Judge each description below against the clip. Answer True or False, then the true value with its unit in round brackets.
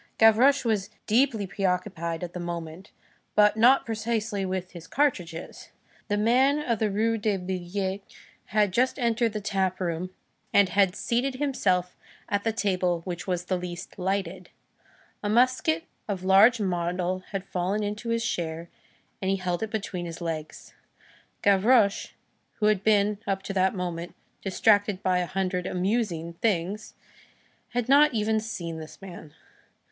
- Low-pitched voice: False (195 Hz)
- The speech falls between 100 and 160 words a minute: True (150 wpm)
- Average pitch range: True (3.4 semitones)